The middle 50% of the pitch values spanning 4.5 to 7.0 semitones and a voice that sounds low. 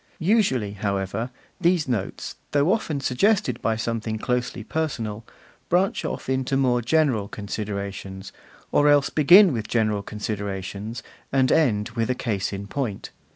Yes: wide, 5.5 semitones; low, 115 Hz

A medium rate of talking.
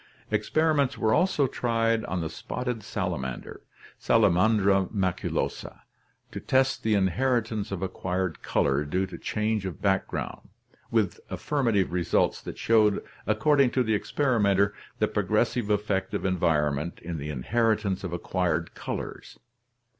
No: slow, 130 wpm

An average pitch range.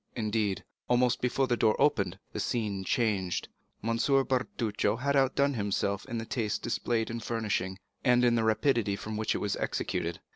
Yes: average, 3.1 semitones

